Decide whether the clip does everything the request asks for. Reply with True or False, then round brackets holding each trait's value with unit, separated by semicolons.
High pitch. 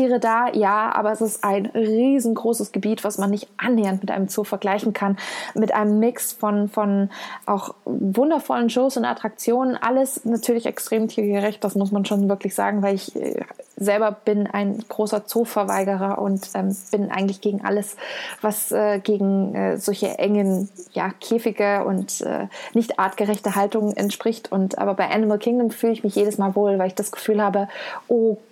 True (210 Hz)